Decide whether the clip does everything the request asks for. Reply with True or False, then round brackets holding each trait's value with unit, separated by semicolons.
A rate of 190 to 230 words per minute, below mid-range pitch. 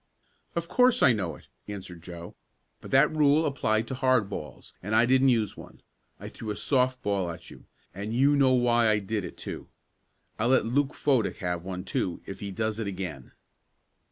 True (195 wpm; 110 Hz)